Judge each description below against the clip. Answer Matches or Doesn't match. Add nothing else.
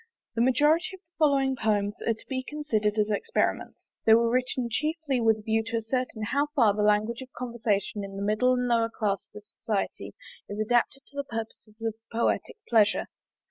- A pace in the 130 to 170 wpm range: Doesn't match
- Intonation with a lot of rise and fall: Doesn't match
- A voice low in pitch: Doesn't match